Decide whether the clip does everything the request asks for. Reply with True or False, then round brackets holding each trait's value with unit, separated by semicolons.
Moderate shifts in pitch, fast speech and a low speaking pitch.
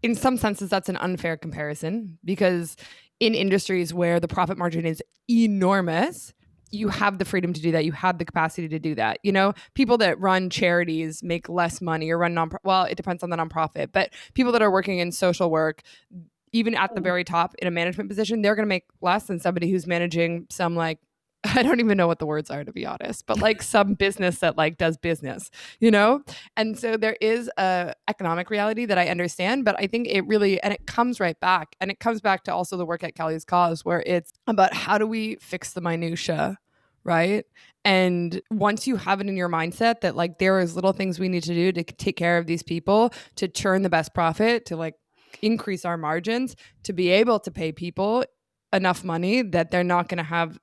False (3.5 semitones; 220 wpm; 185 Hz)